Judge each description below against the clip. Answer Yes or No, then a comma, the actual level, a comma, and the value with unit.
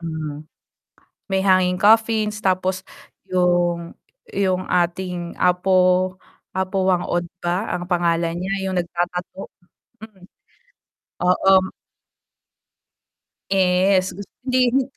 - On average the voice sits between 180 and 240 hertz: Yes, medium, 185 Hz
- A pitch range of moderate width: No, narrow, 1.5 semitones